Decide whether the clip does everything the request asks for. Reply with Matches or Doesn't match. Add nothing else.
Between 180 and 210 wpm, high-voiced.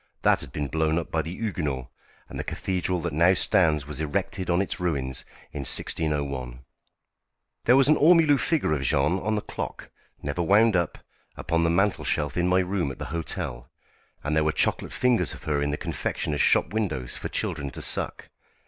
Doesn't match